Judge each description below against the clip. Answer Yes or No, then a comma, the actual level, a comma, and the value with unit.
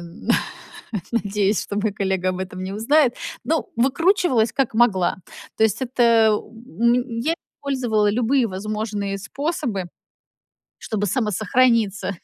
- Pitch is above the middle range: Yes, high, 220 Hz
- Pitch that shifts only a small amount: No, average, 3.8 semitones